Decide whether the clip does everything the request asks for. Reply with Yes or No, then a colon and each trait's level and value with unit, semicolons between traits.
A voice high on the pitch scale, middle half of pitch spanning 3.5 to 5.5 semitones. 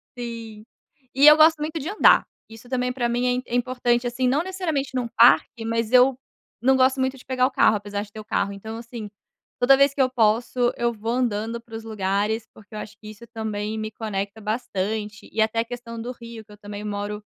No: high, 230 Hz; average, 2.9 semitones